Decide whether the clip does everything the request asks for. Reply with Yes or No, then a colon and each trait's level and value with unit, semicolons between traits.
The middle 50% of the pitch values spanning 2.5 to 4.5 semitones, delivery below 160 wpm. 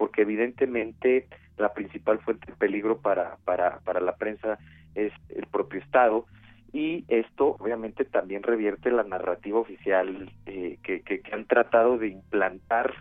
Yes: average, 3.3 semitones; average, 150 wpm